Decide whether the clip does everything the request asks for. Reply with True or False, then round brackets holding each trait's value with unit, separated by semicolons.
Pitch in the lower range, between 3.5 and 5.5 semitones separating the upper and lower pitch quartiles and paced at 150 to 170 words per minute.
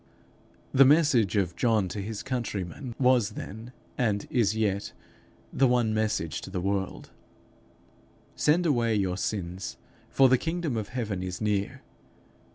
False (110 Hz; 4.3 semitones; 140 wpm)